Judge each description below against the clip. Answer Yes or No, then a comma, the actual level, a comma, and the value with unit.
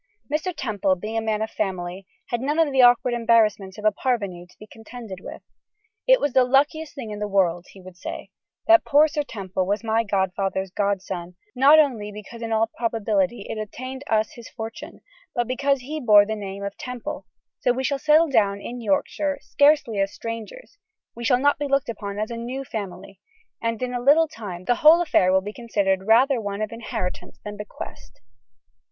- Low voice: No, high, 225 Hz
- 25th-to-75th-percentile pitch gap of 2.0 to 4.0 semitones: No, average, 4.7 semitones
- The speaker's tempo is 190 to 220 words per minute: Yes, average, 195 wpm